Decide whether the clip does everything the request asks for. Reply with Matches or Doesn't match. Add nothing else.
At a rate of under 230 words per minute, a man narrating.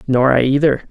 Matches